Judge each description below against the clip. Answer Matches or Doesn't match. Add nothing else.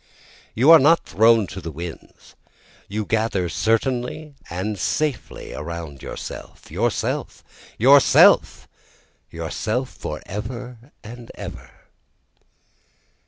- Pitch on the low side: Matches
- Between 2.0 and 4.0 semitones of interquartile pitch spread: Doesn't match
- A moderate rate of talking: Doesn't match